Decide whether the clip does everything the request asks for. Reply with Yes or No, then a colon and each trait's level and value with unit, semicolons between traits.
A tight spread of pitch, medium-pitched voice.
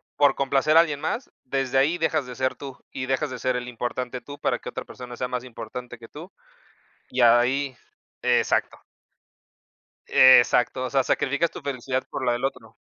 No: narrow, 2.1 semitones; low, 130 Hz